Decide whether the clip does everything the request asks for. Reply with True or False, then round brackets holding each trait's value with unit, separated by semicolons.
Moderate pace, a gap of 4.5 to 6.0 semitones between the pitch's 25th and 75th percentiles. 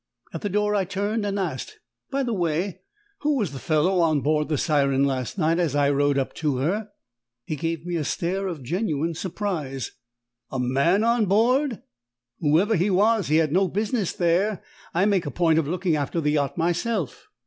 True (190 wpm; 5.2 semitones)